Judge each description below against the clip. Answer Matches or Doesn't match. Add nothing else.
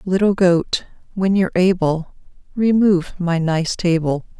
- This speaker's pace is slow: Matches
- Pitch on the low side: Doesn't match